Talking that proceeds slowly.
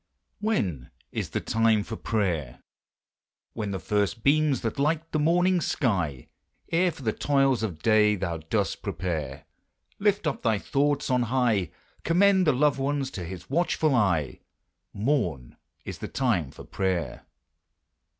No: average, 145 wpm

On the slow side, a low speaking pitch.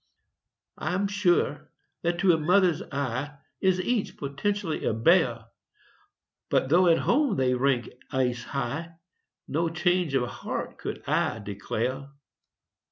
No: slow, 125 wpm; medium, 155 Hz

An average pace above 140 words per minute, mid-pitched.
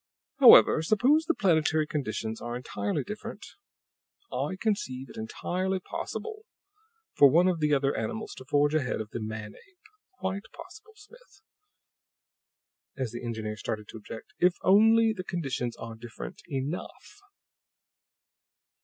No: slow, 135 wpm; medium, 155 Hz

